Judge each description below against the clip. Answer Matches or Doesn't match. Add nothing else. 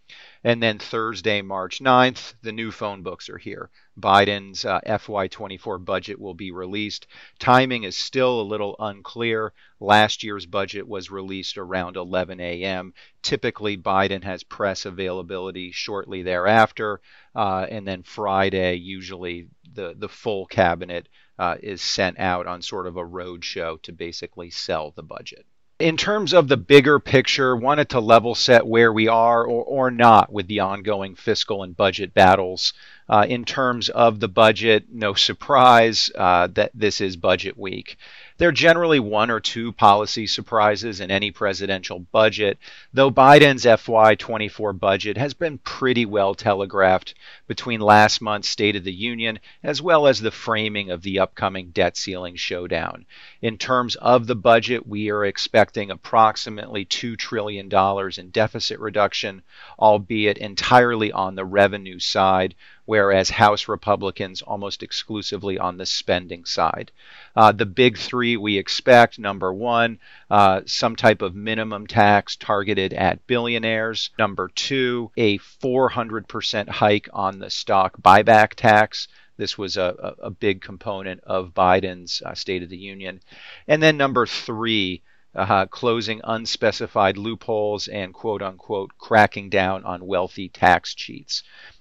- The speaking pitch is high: Doesn't match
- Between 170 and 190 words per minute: Doesn't match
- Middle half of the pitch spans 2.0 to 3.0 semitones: Doesn't match